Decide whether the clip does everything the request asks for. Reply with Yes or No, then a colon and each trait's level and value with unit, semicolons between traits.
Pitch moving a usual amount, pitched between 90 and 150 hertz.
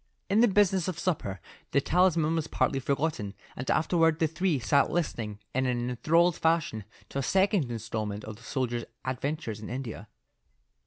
No: wide, 6.0 semitones; medium, 140 Hz